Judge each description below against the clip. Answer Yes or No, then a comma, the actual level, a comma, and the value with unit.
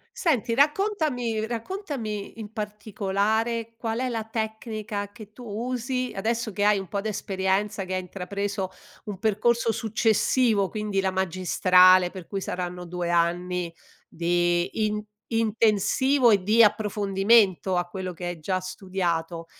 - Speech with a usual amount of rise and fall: Yes, average, 3.4 semitones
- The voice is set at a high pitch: Yes, high, 205 Hz